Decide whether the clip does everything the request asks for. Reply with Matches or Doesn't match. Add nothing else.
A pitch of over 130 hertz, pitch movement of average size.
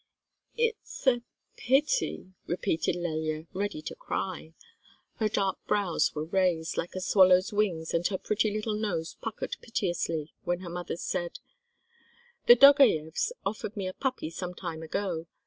Matches